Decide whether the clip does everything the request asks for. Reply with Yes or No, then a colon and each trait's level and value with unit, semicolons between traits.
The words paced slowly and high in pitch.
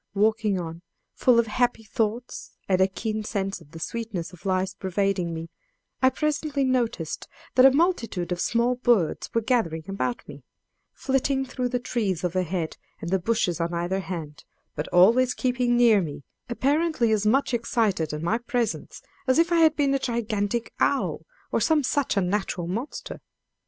No: average, 165 wpm; high, 220 Hz